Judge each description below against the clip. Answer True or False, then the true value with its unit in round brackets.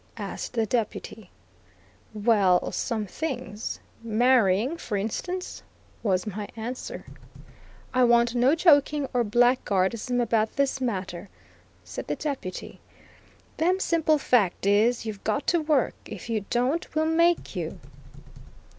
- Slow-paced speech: True (120 wpm)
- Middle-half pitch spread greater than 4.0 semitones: True (5.1 semitones)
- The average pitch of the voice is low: False (240 Hz)